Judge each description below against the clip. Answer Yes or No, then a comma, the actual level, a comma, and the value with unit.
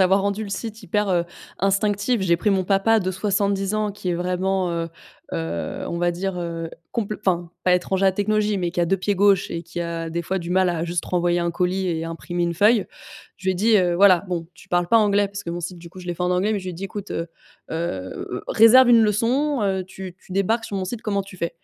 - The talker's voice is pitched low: No, medium, 185 Hz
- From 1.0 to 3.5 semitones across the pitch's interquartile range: Yes, average, 2.7 semitones